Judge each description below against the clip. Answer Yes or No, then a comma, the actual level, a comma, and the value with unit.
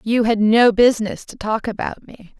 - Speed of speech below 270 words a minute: Yes, average, 200 wpm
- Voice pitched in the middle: No, high, 220 Hz